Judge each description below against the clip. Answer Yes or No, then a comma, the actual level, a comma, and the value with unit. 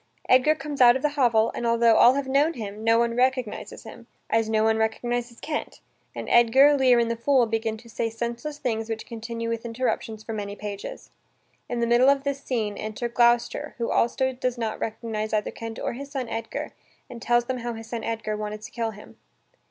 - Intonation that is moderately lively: No, narrow, 2.3 semitones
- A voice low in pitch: No, high, 235 Hz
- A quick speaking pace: Yes, fast, 210 wpm